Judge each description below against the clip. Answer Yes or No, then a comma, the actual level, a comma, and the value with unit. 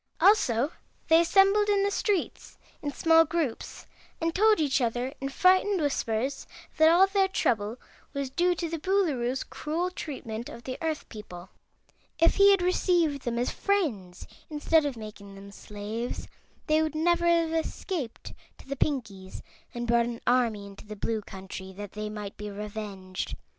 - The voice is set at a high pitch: Yes, very high, 275 Hz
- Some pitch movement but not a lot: No, wide, 7.8 semitones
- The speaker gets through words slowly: No, average, 165 wpm